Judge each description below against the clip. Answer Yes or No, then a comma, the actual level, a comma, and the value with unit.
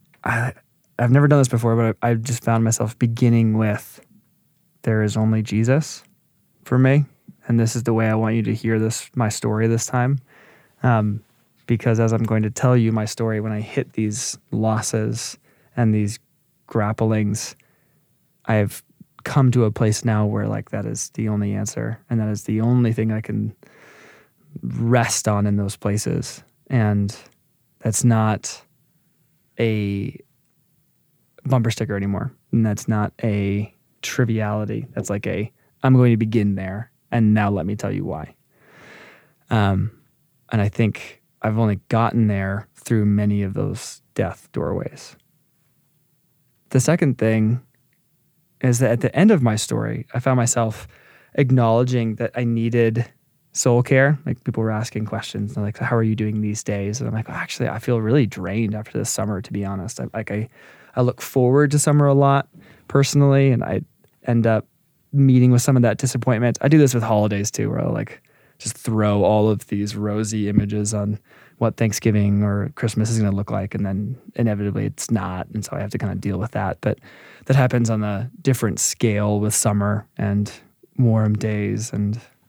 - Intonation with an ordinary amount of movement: Yes, average, 3.5 semitones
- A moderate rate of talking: Yes, average, 175 wpm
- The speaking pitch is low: Yes, low, 115 Hz